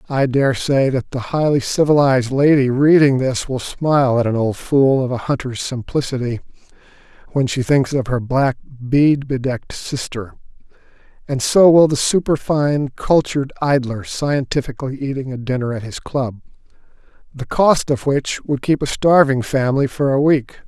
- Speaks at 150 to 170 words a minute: Yes, average, 160 wpm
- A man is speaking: Yes, male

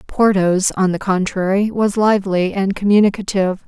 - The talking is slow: Yes, slow, 130 wpm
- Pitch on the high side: Yes, high, 195 Hz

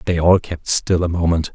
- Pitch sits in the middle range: No, very low, 85 Hz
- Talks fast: Yes, fast, 235 wpm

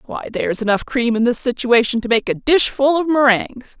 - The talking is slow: No, fast, 205 wpm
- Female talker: Yes, female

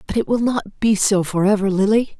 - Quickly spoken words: Yes, fast, 245 wpm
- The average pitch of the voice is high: Yes, high, 205 Hz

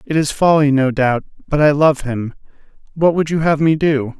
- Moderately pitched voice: Yes, medium, 145 Hz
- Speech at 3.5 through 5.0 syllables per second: Yes, 4.9 syllables/s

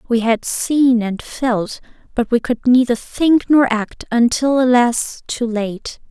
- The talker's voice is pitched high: Yes, high, 240 Hz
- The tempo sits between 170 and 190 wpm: No, average, 155 wpm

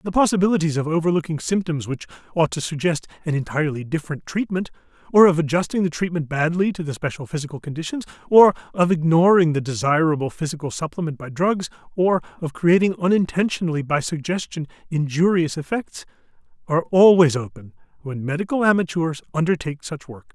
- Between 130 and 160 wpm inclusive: Yes, average, 145 wpm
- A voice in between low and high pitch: Yes, medium, 165 Hz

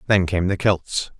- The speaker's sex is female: No, male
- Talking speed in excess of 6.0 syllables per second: No, 4.1 syllables/s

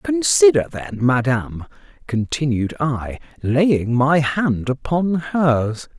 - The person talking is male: Yes, male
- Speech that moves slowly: Yes, slow, 100 wpm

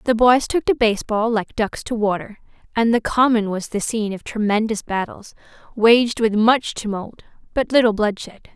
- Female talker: Yes, female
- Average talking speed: Yes, average, 180 wpm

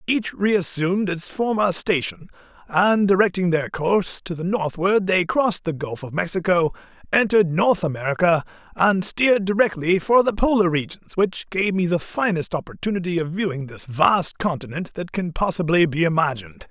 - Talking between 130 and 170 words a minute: Yes, average, 160 wpm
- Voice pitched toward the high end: No, medium, 180 Hz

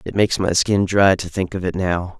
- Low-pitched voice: Yes, very low, 95 Hz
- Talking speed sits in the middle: No, fast, 275 wpm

